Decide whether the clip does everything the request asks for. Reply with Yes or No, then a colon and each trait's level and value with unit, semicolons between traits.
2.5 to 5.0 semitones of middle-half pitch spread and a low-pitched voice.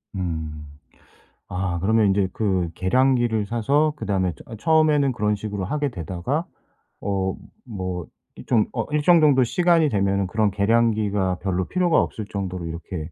No: wide, 5.6 semitones; low, 105 Hz